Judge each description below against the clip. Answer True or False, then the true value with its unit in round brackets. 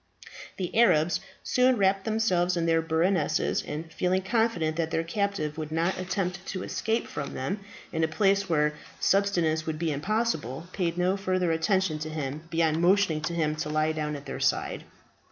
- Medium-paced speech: True (175 wpm)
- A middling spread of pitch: True (3.5 semitones)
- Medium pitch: True (170 Hz)